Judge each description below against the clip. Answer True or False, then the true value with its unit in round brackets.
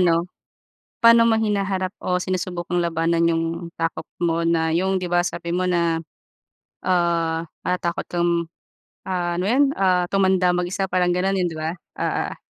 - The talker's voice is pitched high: False (175 Hz)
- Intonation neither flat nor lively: False (1.8 semitones)